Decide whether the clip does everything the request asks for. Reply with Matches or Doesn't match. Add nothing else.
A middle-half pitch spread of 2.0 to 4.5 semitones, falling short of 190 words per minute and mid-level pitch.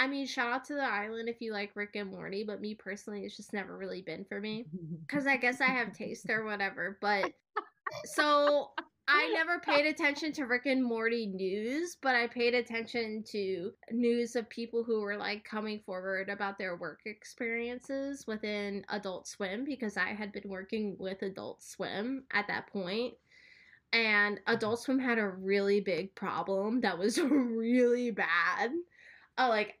Doesn't match